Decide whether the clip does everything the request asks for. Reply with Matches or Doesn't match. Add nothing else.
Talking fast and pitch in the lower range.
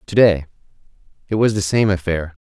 Doesn't match